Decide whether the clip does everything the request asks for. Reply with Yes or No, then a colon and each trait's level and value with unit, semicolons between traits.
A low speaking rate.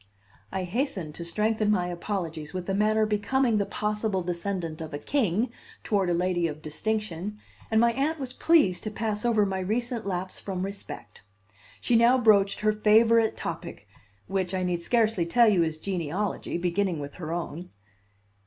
No: average, 170 wpm